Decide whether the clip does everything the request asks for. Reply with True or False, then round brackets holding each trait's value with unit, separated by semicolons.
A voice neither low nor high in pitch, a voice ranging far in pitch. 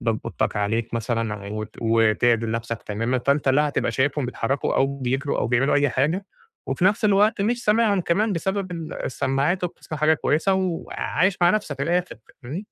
True (145 Hz; 7.6 semitones)